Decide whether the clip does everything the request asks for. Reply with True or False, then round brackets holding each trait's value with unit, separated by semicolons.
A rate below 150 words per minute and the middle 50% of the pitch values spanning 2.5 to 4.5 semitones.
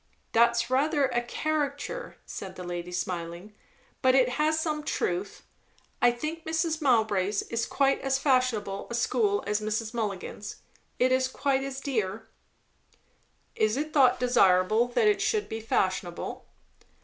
False (140 wpm; 5.2 semitones)